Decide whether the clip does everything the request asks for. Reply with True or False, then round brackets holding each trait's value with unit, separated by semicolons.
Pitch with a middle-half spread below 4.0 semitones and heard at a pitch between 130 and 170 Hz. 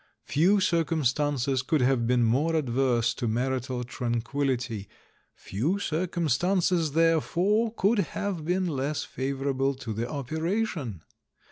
False (5.2 semitones; 140 Hz)